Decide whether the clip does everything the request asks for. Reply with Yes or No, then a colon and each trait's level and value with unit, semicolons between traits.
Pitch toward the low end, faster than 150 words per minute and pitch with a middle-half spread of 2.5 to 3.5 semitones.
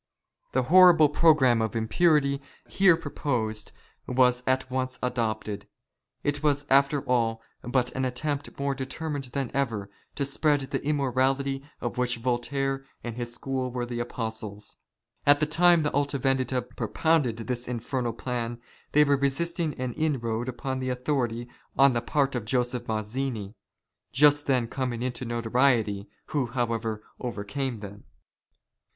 No: low, 130 Hz; average, 145 wpm; average, 2.9 semitones